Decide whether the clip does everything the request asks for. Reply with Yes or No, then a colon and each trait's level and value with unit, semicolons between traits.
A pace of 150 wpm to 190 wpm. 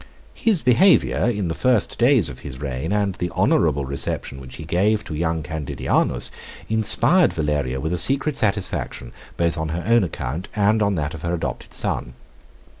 Yes: average, 175 wpm